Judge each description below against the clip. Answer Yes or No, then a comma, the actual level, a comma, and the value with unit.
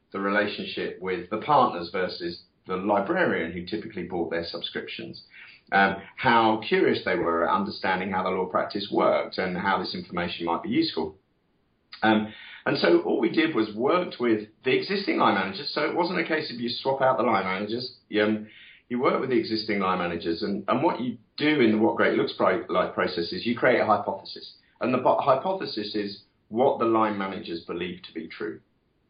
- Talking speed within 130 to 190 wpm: No, average, 200 wpm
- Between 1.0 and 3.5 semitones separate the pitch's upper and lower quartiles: No, average, 4.4 semitones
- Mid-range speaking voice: No, low, 110 Hz